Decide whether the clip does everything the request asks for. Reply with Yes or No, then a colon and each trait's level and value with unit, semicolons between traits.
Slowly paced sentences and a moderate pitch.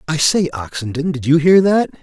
No: fast, 205 wpm; medium, 155 Hz